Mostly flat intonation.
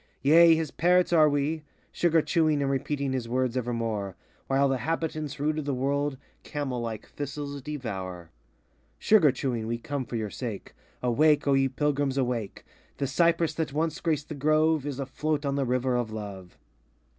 No: average, 3.6 semitones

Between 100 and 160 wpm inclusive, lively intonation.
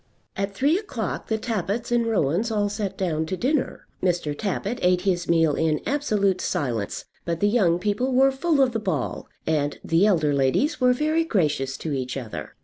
No: average, 185 wpm; wide, 7.0 semitones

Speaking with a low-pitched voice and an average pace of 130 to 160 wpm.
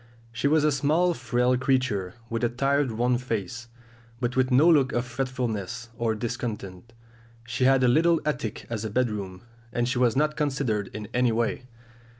No: low, 125 Hz; average, 170 wpm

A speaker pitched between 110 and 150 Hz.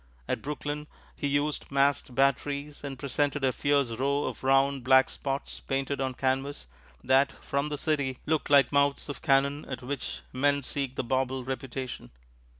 Yes: medium, 140 Hz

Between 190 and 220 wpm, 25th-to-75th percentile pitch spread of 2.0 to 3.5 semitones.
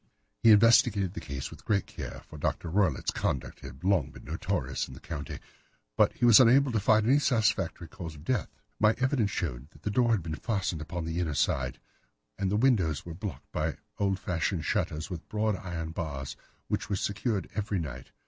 No: average, 195 wpm; average, 5.3 semitones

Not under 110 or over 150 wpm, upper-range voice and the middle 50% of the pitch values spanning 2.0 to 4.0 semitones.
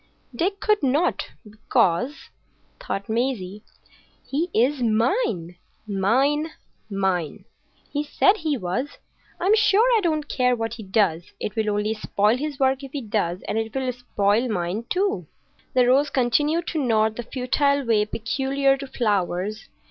No: average, 145 wpm; high, 245 Hz; wide, 5.4 semitones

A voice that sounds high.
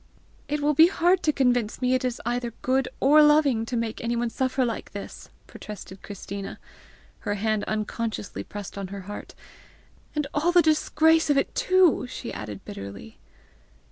Yes: high, 245 Hz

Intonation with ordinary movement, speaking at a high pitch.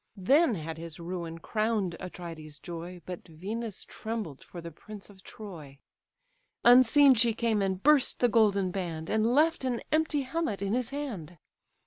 No: wide, 5.8 semitones; high, 200 Hz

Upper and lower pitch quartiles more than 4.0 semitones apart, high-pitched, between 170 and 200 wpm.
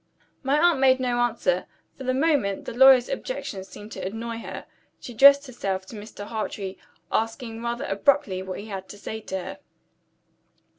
Yes: average, 4.7 semitones; high, 230 Hz; average, 175 wpm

